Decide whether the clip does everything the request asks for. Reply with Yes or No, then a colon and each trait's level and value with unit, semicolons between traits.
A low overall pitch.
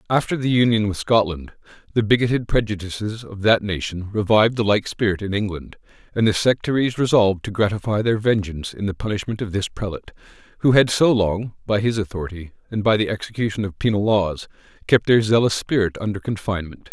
Yes: low, 105 Hz